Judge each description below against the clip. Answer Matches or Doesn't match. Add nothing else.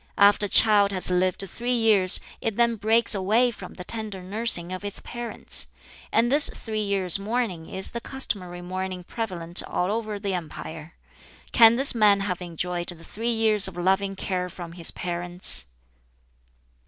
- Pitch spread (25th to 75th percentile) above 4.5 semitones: Doesn't match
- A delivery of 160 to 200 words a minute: Matches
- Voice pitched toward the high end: Matches